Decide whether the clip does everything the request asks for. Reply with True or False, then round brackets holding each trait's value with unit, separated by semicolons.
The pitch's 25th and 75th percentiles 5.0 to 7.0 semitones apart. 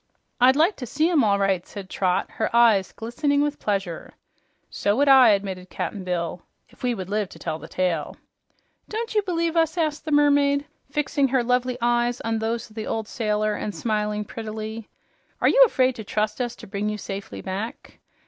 True (5.5 semitones)